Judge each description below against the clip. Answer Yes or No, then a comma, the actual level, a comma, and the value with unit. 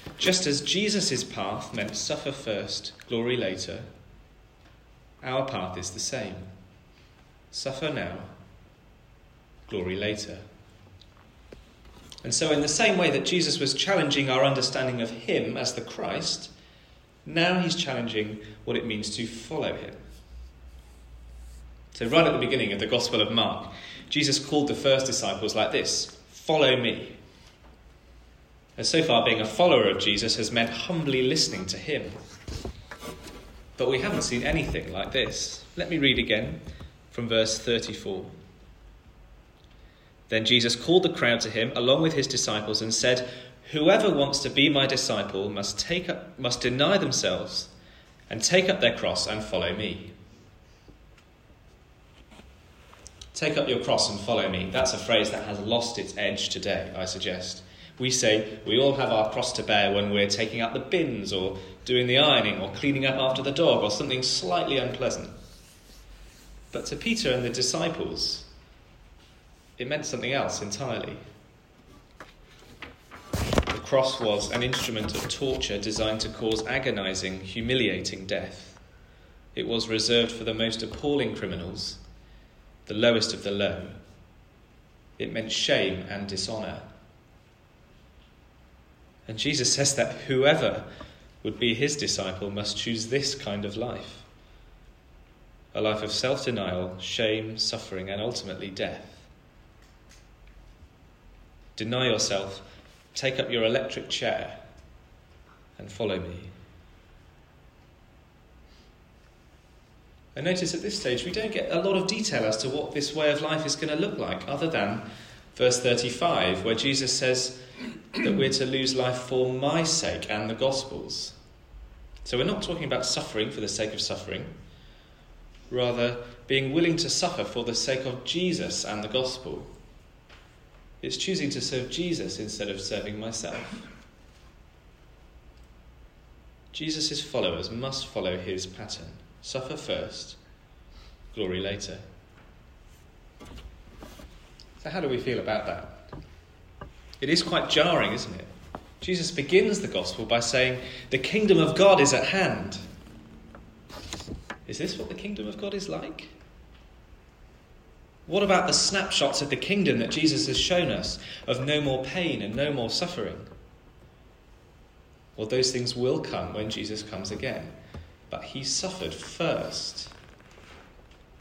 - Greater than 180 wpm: No, average, 140 wpm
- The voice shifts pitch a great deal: Yes, wide, 6.0 semitones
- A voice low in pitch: Yes, low, 115 Hz